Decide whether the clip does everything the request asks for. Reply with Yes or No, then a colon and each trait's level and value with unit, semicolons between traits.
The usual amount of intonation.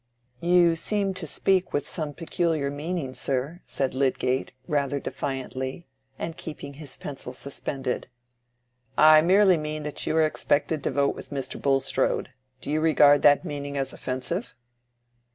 Yes: average, 3.2 semitones